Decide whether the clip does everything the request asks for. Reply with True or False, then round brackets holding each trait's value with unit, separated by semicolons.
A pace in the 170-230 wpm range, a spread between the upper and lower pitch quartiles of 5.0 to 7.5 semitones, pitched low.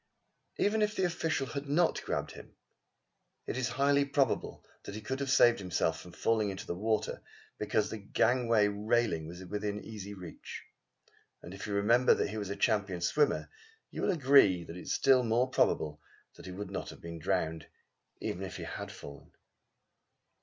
True (180 wpm; 5.6 semitones; 105 Hz)